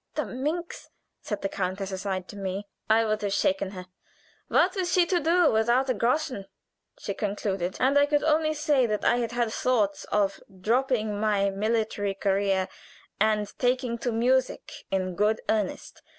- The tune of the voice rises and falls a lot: No, average, 4.5 semitones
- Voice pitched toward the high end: Yes, high, 220 Hz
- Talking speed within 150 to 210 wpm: Yes, average, 165 wpm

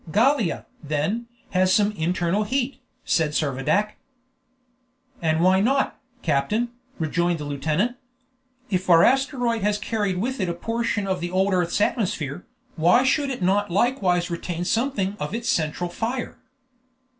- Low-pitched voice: No, high, 190 Hz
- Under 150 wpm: Yes, average, 140 wpm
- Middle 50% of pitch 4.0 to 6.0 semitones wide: Yes, average, 5.1 semitones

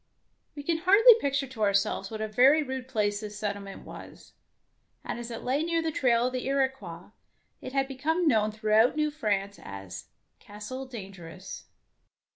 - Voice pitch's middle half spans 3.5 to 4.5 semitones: No, average, 5.0 semitones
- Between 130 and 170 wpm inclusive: Yes, average, 165 wpm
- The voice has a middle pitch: No, high, 240 Hz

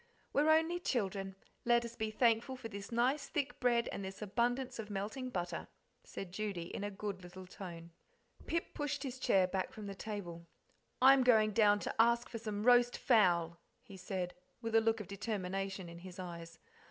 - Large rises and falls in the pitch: No, average, 4.2 semitones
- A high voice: Yes, high, 210 Hz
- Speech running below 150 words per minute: No, average, 185 wpm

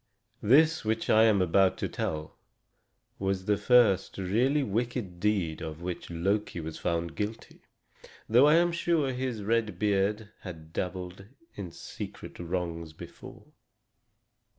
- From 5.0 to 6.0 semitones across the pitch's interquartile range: No, average, 4.6 semitones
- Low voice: Yes, low, 100 Hz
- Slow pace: Yes, slow, 130 wpm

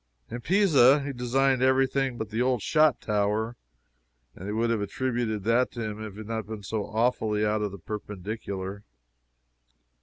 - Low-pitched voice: Yes, low, 110 Hz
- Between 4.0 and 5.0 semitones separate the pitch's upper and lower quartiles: No, average, 3.3 semitones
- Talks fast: No, average, 180 wpm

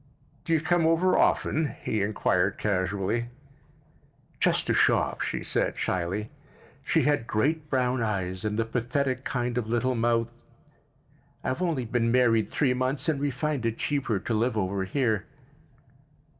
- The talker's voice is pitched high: No, low, 120 Hz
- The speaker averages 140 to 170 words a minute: Yes, average, 150 wpm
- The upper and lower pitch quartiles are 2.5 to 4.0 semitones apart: No, average, 4.5 semitones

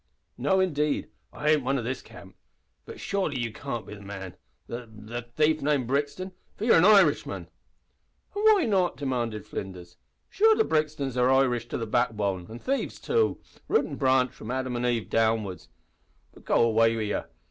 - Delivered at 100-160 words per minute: No, average, 180 wpm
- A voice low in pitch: Yes, low, 125 Hz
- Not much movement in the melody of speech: No, average, 5.3 semitones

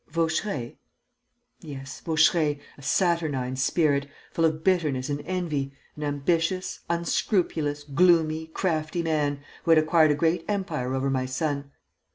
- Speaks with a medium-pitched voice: Yes, medium, 155 Hz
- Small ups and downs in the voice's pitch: No, average, 3.0 semitones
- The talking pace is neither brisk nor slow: No, slow, 130 wpm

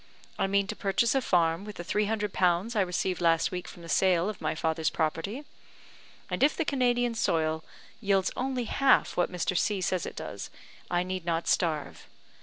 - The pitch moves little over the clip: No, average, 4.2 semitones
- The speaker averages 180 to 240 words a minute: Yes, average, 195 wpm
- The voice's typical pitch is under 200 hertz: Yes, medium, 185 Hz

